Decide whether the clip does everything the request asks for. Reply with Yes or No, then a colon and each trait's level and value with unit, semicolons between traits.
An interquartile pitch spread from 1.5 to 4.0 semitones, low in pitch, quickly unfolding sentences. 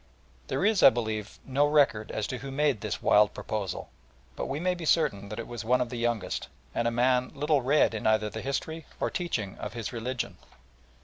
No: average, 4.6 semitones; low, 120 Hz; fast, 210 wpm